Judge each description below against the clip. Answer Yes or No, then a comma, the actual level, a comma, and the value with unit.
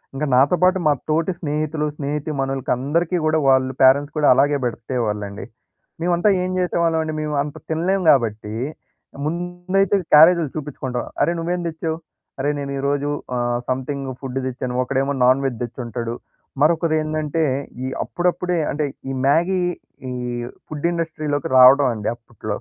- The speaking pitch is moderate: Yes, medium, 145 Hz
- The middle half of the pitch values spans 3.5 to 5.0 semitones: Yes, average, 4.0 semitones